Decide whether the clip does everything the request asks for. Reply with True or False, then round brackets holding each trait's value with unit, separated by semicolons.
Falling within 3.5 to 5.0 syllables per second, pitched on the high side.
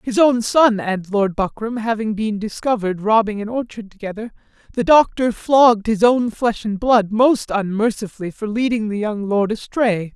True (4.8 syllables/s; 220 Hz)